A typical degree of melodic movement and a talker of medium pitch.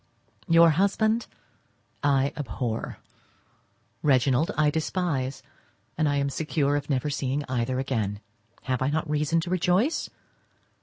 Yes: average, 3.8 semitones; medium, 145 Hz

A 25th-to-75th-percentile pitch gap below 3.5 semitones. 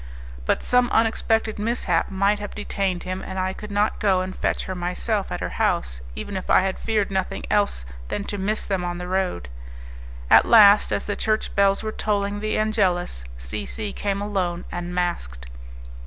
Yes: average, 2.7 semitones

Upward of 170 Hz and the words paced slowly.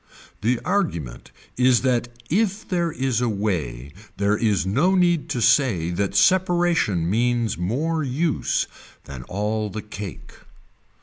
No: low, 115 Hz; slow, 130 wpm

